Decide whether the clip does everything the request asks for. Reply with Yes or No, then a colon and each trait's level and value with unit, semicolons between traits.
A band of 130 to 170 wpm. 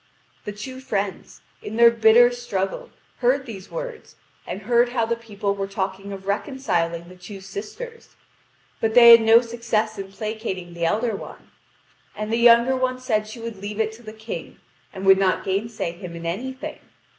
No: average, 180 wpm